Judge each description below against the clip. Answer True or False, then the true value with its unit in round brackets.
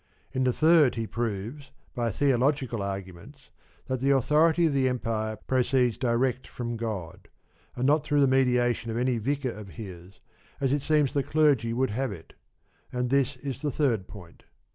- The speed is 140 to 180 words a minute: True (170 wpm)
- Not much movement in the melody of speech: False (3.5 semitones)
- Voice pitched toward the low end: True (125 Hz)